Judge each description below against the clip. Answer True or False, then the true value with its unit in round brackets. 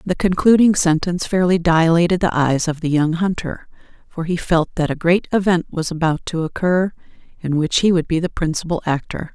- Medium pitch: True (170 Hz)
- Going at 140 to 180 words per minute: False (195 wpm)